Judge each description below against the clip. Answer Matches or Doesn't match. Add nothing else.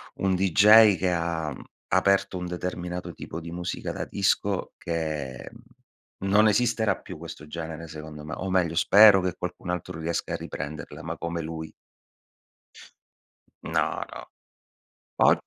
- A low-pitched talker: Matches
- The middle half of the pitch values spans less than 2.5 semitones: Doesn't match